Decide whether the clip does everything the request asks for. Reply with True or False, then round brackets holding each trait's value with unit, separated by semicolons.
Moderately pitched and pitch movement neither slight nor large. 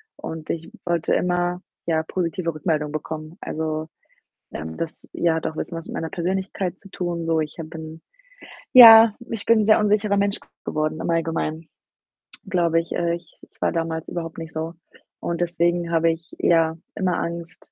False (165 Hz; 1.8 semitones)